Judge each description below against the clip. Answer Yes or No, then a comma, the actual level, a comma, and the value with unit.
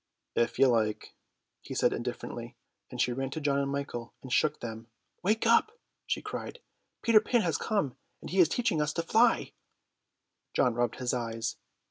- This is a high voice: No, medium, 140 Hz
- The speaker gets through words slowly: No, average, 180 wpm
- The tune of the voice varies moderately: No, wide, 8.2 semitones